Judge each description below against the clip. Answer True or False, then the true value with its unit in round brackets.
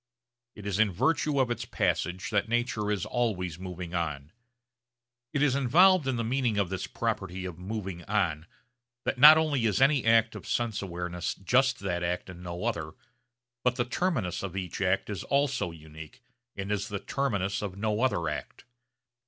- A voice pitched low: True (105 Hz)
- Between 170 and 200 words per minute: True (175 wpm)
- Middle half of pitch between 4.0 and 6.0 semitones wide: True (5.6 semitones)